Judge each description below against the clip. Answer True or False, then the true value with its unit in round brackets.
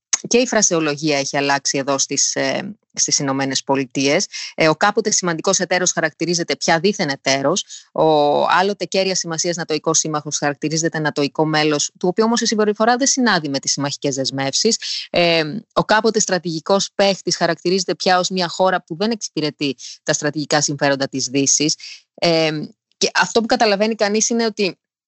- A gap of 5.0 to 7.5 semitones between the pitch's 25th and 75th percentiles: True (5.5 semitones)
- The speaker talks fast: False (150 wpm)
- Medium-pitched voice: True (165 Hz)